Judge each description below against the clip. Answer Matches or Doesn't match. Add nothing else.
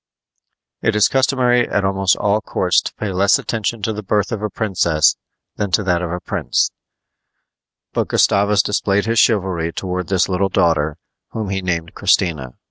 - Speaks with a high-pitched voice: Doesn't match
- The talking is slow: Doesn't match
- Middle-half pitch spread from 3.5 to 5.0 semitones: Doesn't match